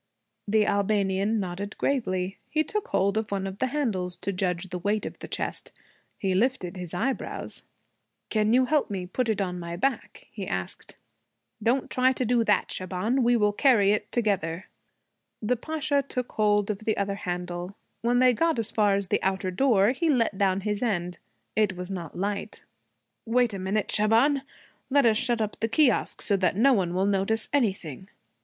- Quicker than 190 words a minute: No, average, 185 wpm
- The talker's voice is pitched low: No, high, 210 Hz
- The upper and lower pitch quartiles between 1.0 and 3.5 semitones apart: No, average, 4.2 semitones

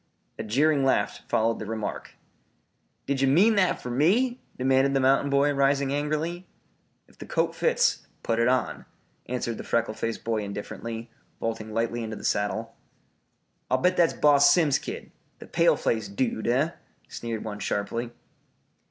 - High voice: No, low, 130 Hz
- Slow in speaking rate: No, average, 160 wpm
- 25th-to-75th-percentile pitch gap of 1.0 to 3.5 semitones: No, average, 4.4 semitones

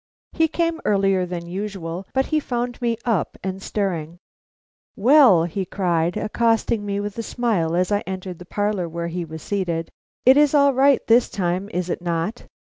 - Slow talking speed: No, average, 180 wpm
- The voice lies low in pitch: No, high, 195 Hz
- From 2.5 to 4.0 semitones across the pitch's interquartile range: No, average, 5.1 semitones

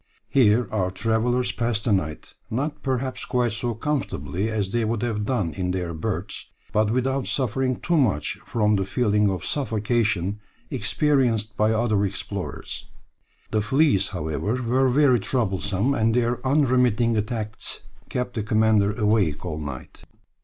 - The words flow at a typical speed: Yes, average, 145 wpm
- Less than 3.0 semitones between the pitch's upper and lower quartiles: No, average, 3.5 semitones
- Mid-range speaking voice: No, low, 110 Hz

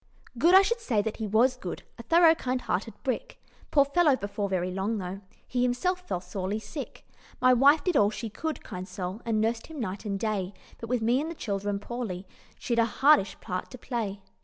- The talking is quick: Yes, fast, 210 wpm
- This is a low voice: No, high, 230 Hz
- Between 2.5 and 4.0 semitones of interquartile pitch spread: No, wide, 5.6 semitones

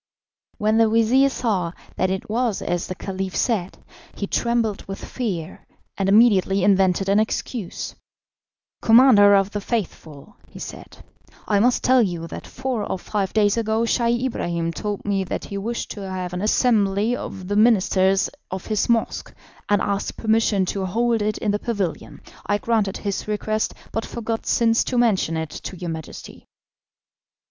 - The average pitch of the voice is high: Yes, high, 205 Hz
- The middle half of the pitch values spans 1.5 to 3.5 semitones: Yes, average, 3.1 semitones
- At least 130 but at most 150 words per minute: No, average, 165 wpm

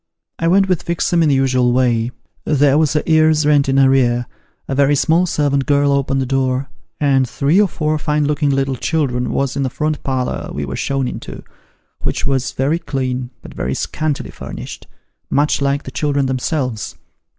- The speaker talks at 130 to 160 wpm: No, average, 185 wpm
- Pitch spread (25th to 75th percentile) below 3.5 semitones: Yes, narrow, 2.5 semitones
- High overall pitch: No, medium, 140 Hz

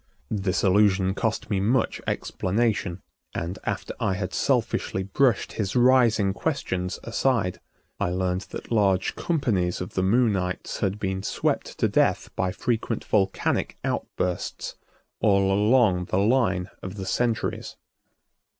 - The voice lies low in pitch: Yes, low, 100 Hz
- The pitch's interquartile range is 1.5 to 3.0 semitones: No, average, 3.4 semitones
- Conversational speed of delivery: No, slow, 130 wpm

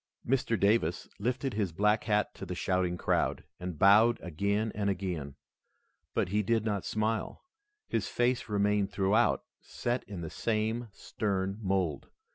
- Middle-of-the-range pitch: No, low, 105 Hz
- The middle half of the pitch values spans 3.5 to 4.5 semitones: No, average, 2.8 semitones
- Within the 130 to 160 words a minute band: Yes, average, 145 wpm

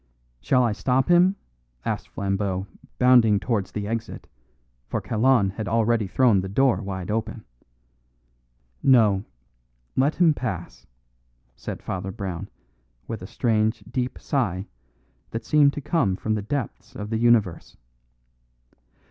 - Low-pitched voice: Yes, low, 110 Hz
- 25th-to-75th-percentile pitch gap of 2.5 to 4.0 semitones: No, average, 4.5 semitones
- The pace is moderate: No, slow, 130 wpm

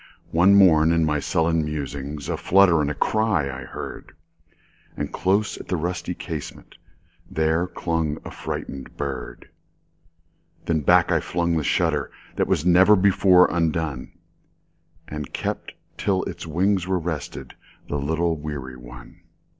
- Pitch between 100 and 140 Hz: No, very low, 80 Hz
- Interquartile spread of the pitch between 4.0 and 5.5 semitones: No, narrow, 2.6 semitones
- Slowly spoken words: Yes, slow, 120 wpm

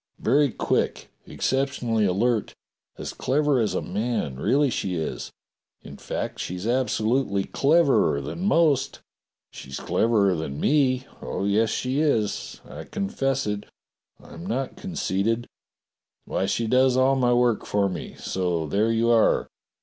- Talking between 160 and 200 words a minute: No, average, 140 wpm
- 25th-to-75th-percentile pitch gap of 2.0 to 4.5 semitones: No, average, 5.1 semitones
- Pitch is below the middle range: Yes, low, 115 Hz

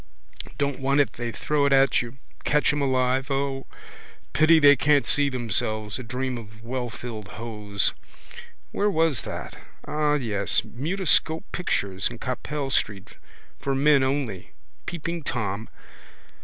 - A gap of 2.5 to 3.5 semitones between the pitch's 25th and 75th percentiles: No, average, 4.1 semitones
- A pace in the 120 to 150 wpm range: Yes, slow, 135 wpm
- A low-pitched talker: Yes, low, 130 Hz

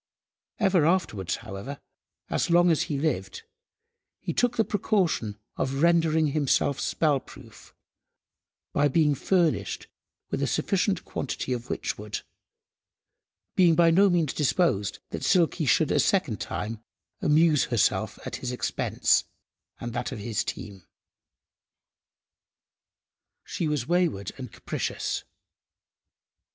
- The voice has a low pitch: No, medium, 150 Hz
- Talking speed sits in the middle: No, slow, 115 wpm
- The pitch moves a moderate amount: No, wide, 6.3 semitones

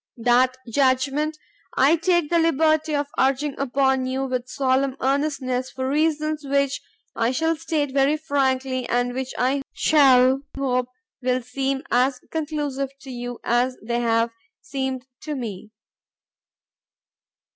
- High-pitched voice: Yes, very high, 265 Hz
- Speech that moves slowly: Yes, slow, 130 wpm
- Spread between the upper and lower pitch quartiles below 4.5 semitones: Yes, narrow, 2.4 semitones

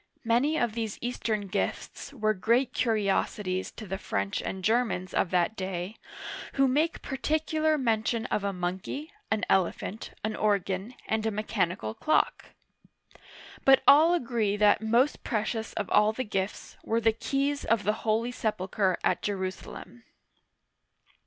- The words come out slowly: No, average, 145 wpm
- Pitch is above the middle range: Yes, high, 220 Hz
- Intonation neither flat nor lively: Yes, average, 4.0 semitones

